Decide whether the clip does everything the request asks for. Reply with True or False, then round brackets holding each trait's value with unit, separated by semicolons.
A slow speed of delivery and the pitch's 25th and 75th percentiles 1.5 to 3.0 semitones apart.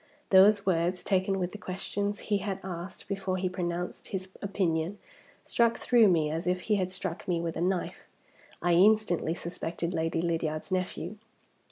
False (165 wpm; 2.4 semitones)